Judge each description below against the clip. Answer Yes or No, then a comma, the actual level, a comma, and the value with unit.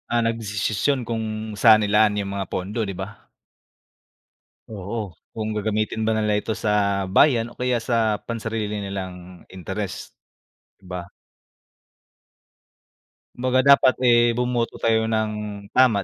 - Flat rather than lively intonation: Yes, narrow, 2.3 semitones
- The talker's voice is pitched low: Yes, low, 110 Hz